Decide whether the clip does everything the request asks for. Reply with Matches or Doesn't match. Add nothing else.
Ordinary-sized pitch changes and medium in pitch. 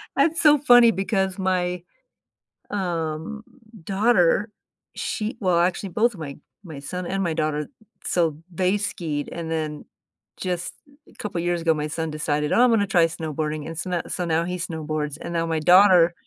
Matches